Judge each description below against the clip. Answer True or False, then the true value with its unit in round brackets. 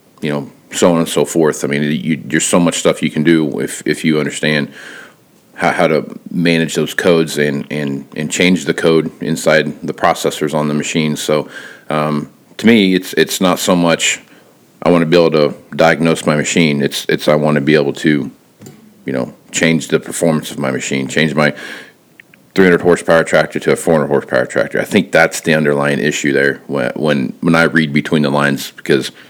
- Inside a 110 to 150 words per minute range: False (200 wpm)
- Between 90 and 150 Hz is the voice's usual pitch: False (80 Hz)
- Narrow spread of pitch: True (2.1 semitones)